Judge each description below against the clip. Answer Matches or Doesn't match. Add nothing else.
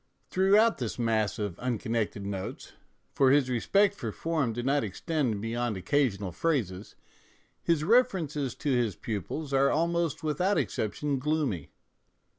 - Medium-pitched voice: Doesn't match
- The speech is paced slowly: Matches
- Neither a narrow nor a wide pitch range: Doesn't match